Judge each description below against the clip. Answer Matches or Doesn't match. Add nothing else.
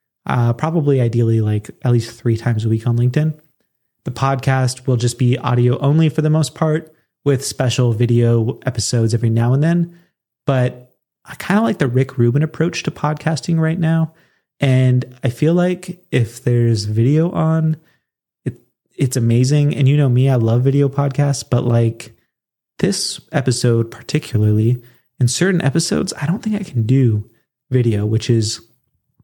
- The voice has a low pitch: Matches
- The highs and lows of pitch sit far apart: Doesn't match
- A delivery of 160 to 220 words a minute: Matches